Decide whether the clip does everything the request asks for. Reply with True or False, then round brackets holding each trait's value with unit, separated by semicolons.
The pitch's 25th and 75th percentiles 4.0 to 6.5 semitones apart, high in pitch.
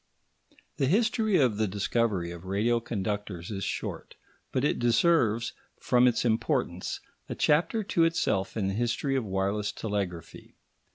False (5.1 semitones; 115 Hz)